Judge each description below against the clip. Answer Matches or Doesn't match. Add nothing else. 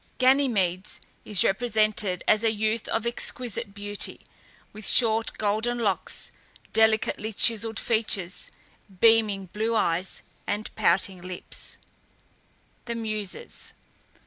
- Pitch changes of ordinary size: Doesn't match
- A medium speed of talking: Doesn't match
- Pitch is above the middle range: Matches